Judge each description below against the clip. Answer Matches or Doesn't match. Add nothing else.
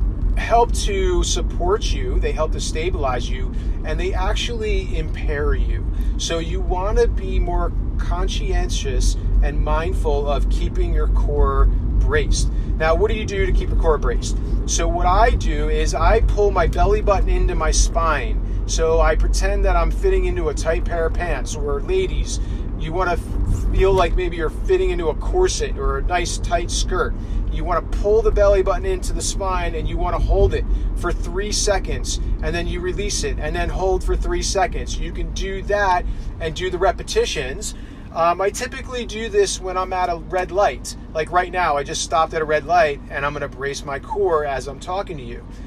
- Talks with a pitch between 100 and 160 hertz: Doesn't match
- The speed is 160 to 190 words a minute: Doesn't match